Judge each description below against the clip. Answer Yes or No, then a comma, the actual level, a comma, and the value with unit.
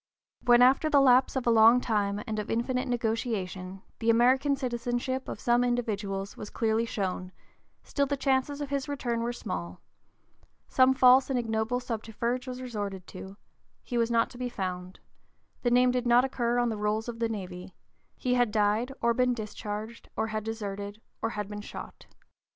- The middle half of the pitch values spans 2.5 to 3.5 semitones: Yes, average, 3.0 semitones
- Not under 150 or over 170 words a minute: No, average, 180 wpm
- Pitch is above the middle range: Yes, high, 235 Hz